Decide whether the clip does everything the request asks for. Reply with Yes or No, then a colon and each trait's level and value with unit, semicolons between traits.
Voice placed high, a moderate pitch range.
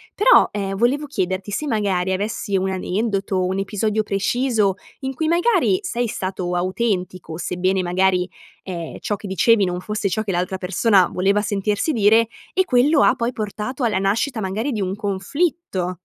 Yes: high, 205 Hz; average, 3.9 semitones